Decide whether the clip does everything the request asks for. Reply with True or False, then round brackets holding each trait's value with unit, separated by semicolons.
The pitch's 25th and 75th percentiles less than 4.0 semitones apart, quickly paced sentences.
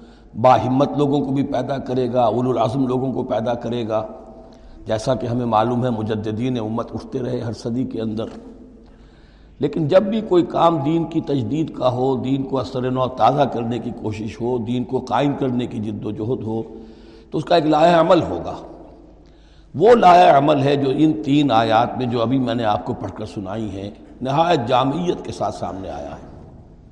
True (3.4 semitones; 200 wpm)